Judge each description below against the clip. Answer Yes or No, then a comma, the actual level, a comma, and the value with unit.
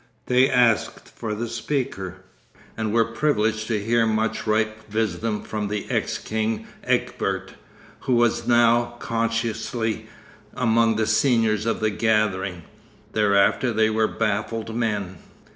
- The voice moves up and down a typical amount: No, narrow, 1.3 semitones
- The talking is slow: Yes, slow, 125 wpm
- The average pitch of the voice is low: Yes, low, 110 Hz